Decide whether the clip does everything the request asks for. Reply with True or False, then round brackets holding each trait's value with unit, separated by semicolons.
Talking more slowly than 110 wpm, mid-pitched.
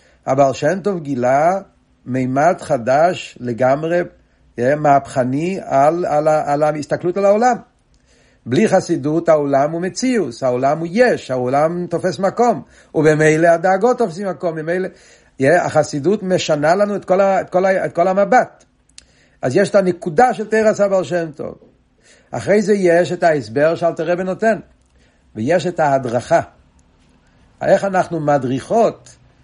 False (140 wpm; 170 Hz)